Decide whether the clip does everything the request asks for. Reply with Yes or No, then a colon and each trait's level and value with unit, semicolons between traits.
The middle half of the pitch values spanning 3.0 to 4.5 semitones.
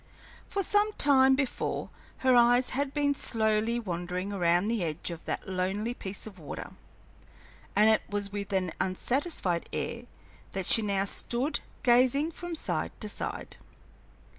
No: wide, 5.6 semitones